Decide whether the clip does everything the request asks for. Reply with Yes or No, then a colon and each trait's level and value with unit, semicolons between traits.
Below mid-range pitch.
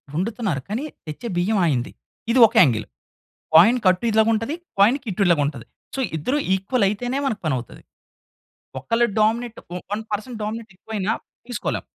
No: high, 215 Hz